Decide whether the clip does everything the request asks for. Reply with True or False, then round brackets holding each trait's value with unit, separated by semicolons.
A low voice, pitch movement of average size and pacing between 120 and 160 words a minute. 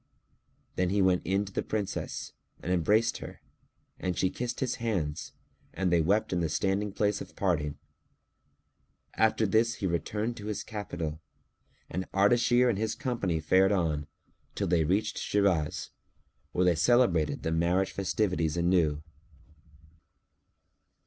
True (95 Hz; 3.9 semitones; 140 wpm)